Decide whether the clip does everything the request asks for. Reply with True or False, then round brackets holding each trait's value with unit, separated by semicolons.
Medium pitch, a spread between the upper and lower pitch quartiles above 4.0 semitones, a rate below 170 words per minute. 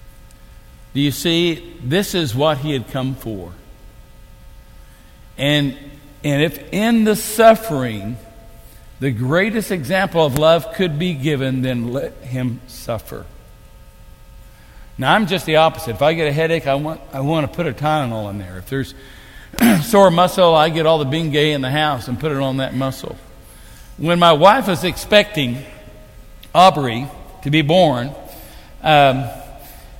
True (145 Hz; 4.7 semitones; 150 wpm)